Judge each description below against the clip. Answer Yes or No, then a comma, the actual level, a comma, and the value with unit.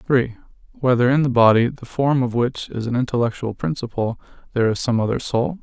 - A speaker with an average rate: Yes, average, 190 wpm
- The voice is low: Yes, low, 125 Hz